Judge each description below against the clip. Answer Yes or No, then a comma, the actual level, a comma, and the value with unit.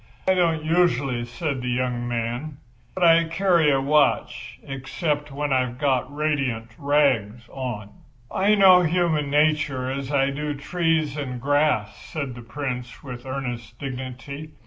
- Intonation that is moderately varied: Yes, average, 3.5 semitones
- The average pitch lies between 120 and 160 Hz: Yes, medium, 140 Hz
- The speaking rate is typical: Yes, average, 145 wpm